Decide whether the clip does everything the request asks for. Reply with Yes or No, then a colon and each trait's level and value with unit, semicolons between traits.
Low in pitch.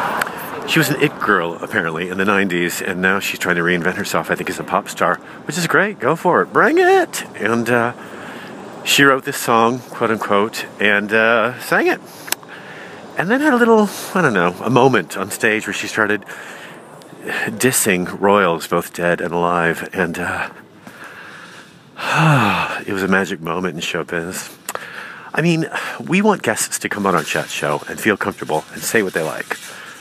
Yes: low, 110 Hz